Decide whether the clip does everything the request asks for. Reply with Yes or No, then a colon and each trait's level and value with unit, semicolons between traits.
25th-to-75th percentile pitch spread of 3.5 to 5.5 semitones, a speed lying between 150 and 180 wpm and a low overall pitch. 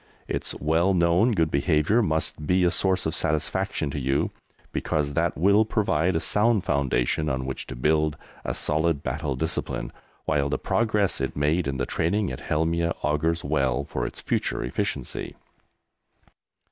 Yes: average, 4.1 semitones; average, 160 wpm; very low, 80 Hz